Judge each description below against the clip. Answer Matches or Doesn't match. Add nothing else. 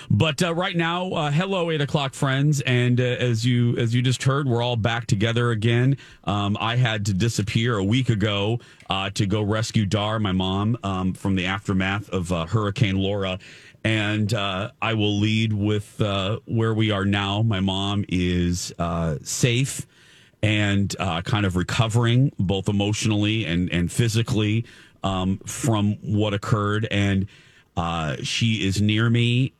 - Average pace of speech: Matches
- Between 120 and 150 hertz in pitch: Doesn't match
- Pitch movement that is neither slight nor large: Matches